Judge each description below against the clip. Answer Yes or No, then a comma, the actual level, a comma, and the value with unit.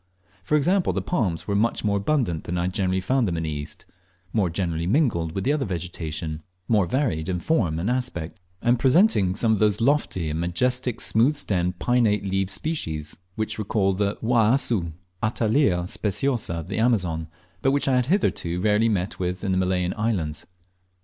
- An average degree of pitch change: No, wide, 5.7 semitones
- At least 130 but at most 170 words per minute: No, average, 185 wpm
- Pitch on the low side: Yes, low, 100 Hz